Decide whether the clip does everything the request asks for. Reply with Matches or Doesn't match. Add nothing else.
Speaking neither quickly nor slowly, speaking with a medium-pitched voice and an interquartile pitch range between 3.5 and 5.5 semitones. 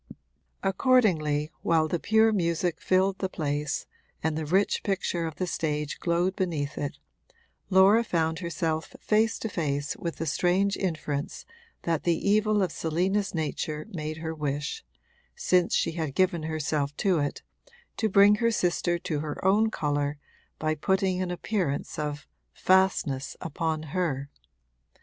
Matches